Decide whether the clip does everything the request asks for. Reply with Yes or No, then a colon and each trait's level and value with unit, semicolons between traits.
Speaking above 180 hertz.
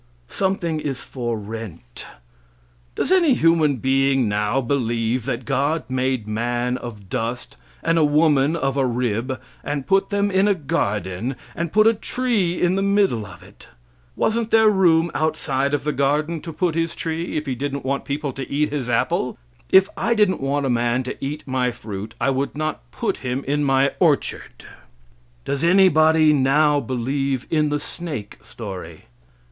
No: medium, 140 Hz